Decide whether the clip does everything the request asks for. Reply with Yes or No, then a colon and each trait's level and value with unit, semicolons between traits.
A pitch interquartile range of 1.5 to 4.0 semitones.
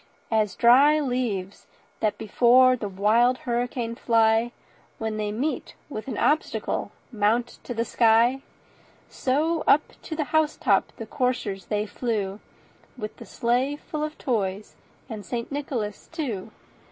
Yes: average, 3.5 semitones